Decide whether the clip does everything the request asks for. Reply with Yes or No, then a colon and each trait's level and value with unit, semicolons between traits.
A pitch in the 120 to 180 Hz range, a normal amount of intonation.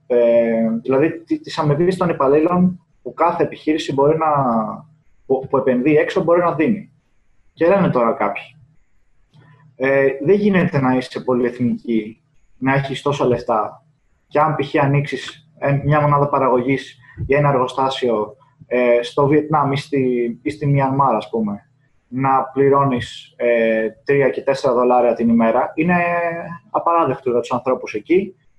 Yes: medium, 140 Hz; average, 3.6 semitones